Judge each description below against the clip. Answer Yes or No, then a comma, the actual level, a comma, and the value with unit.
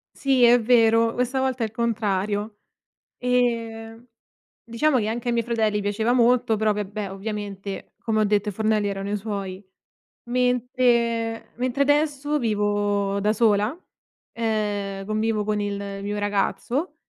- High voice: Yes, high, 220 Hz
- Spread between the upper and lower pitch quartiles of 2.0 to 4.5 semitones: Yes, average, 2.8 semitones